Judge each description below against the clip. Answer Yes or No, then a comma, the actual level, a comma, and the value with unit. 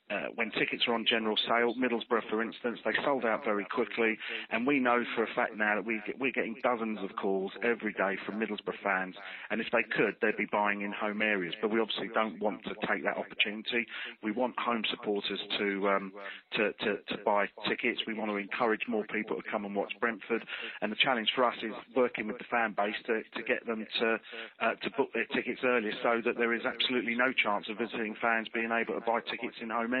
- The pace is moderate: No, fast, 230 wpm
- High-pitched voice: No, low, 110 Hz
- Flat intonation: Yes, narrow, 2.3 semitones